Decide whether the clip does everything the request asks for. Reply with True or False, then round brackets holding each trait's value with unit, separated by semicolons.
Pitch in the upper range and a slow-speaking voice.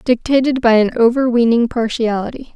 True (235 Hz; 115 wpm)